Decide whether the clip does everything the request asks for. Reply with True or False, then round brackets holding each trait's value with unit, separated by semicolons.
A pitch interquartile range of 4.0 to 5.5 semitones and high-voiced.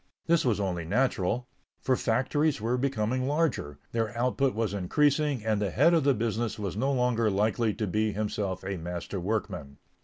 False (4.4 semitones; 110 Hz)